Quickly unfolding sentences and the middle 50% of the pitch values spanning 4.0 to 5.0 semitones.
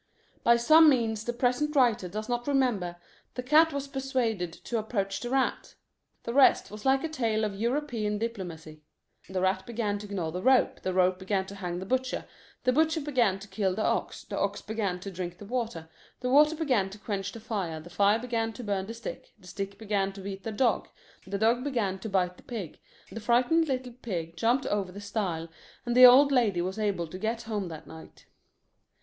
Yes: fast, 210 wpm; average, 4.6 semitones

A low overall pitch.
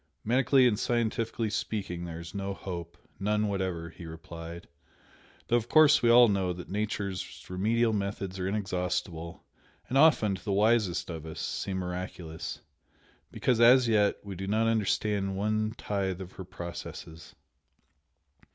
Yes: low, 100 Hz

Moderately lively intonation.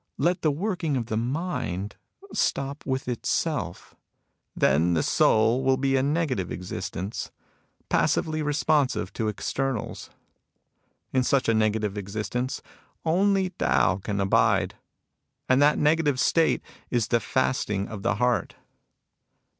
No: wide, 5.9 semitones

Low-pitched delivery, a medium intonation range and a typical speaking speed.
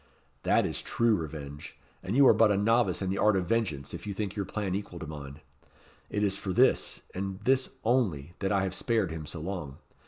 No: very low, 95 Hz; average, 4.6 semitones; fast, 220 wpm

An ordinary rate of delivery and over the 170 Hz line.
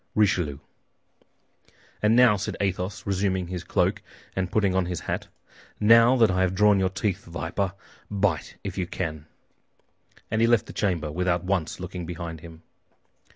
No: average, 155 wpm; very low, 95 Hz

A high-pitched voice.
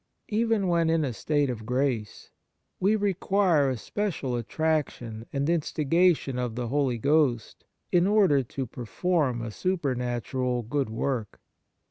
No: medium, 140 Hz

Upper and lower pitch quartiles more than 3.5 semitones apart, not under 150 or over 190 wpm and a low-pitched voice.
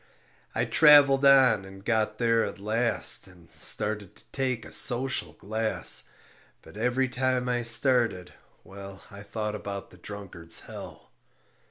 No: average, 3.9 semitones; average, 140 wpm; low, 110 Hz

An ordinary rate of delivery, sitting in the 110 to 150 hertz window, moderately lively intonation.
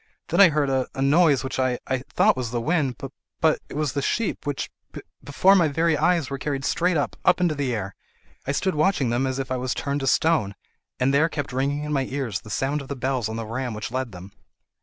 No: fast, 225 wpm; low, 135 Hz; average, 3.0 semitones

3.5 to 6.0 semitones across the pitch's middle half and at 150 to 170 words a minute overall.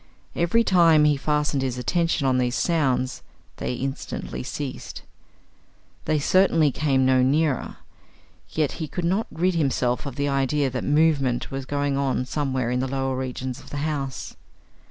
No: average, 3.0 semitones; average, 155 wpm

